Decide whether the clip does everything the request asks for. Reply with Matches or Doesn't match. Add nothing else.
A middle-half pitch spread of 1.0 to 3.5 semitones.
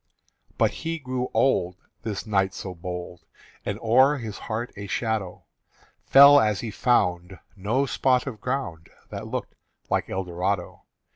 Doesn't match